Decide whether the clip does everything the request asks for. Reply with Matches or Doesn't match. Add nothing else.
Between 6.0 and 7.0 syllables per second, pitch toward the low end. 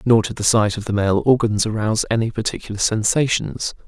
Doesn't match